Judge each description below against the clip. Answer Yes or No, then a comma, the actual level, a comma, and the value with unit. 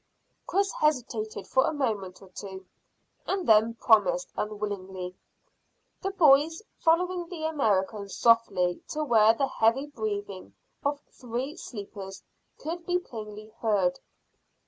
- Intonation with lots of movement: Yes, wide, 7.0 semitones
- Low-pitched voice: No, high, 230 Hz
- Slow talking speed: Yes, slow, 120 wpm